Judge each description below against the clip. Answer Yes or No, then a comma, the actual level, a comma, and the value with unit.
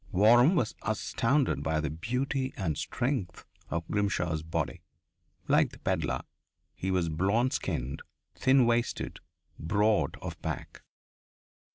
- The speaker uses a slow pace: Yes, slow, 115 wpm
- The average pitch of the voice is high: No, low, 105 Hz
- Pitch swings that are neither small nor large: No, wide, 6.6 semitones